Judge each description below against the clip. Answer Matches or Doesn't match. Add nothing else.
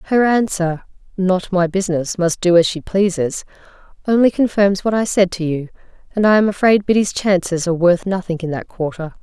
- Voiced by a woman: Matches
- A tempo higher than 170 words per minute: Matches